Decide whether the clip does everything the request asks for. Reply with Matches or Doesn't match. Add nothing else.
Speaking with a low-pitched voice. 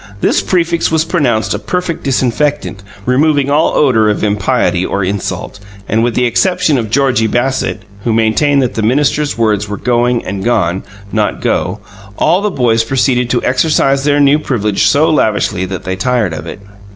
Matches